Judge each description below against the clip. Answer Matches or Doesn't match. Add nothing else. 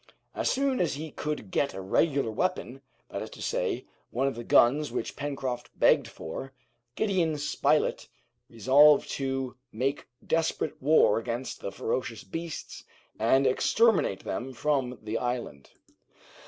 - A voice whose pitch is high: Doesn't match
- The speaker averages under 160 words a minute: Matches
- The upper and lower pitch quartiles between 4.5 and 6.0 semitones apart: Doesn't match